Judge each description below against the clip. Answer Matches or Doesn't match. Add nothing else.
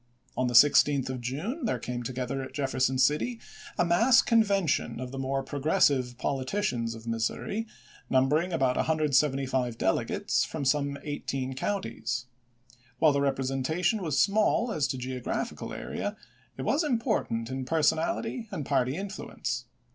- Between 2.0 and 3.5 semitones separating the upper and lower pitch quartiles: Doesn't match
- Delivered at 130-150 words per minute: Matches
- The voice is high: Doesn't match